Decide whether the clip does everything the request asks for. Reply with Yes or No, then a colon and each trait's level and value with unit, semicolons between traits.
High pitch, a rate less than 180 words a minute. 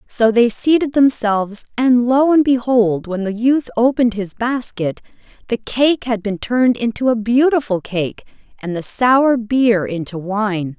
Yes: high, 230 Hz; average, 160 wpm